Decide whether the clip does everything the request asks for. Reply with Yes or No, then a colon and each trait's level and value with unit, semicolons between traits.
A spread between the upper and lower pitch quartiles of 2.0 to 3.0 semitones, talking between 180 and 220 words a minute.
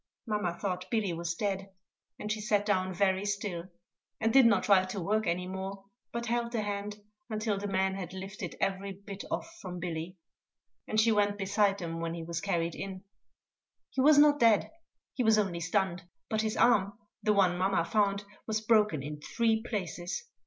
Yes: average, 2.7 semitones; average, 185 wpm